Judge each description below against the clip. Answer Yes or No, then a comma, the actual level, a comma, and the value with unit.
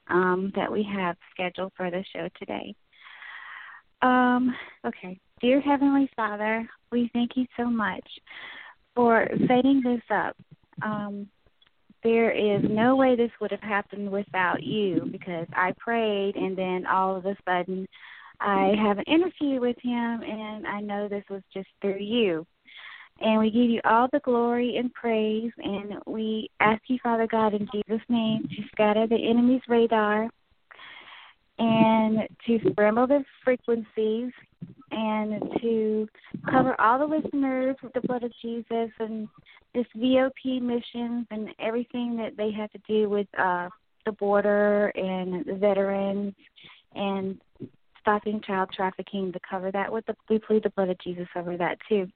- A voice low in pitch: No, high, 215 Hz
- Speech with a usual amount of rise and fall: Yes, average, 3.2 semitones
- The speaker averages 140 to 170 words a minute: Yes, average, 150 wpm